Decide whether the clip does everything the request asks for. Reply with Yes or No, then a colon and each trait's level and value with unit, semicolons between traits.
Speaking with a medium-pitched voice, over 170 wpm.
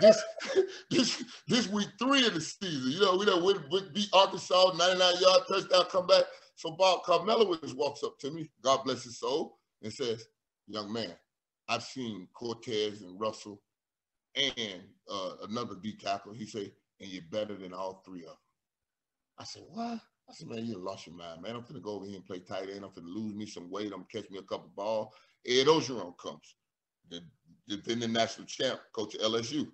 No: low, 130 Hz; fast, 205 wpm